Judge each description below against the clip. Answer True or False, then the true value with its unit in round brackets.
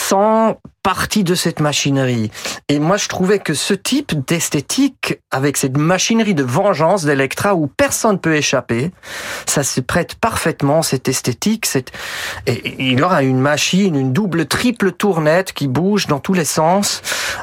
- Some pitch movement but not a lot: False (6.3 semitones)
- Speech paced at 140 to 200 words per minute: True (155 wpm)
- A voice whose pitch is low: False (160 Hz)